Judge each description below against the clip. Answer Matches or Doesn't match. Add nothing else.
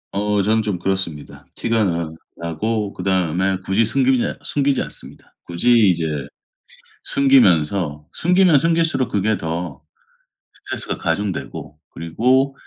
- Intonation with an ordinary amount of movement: Doesn't match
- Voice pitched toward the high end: Doesn't match